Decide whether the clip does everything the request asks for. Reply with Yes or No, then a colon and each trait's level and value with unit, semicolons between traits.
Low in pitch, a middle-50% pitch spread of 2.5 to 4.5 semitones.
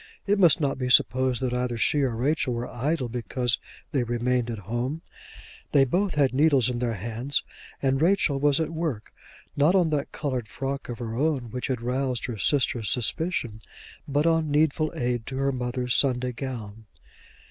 Yes: low, 130 Hz; average, 3.3 semitones